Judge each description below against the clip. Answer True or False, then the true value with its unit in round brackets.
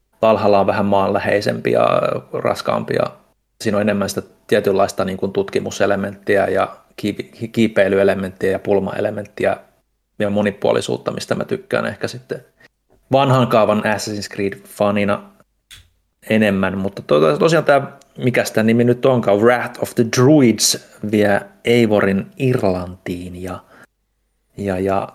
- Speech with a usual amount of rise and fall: False (2.2 semitones)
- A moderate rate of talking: True (120 wpm)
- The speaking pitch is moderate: False (100 Hz)